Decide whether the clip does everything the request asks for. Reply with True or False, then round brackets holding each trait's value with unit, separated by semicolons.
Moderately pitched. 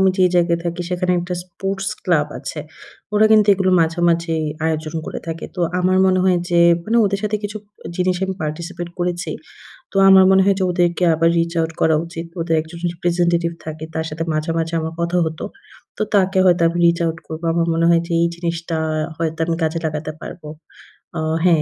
True (170 Hz)